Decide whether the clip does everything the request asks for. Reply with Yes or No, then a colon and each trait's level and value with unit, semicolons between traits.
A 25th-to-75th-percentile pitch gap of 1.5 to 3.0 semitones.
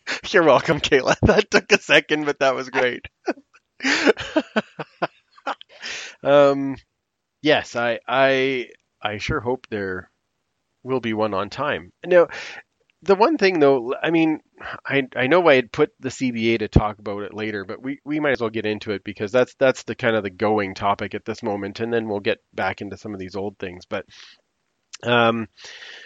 No: average, 4.9 semitones